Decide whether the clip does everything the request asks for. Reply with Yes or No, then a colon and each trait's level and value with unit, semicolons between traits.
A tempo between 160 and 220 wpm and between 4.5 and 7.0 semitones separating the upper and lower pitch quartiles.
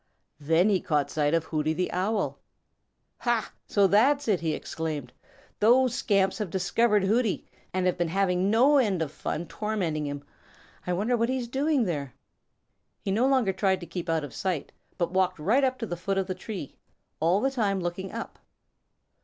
Yes: average, 185 wpm; average, 5.1 semitones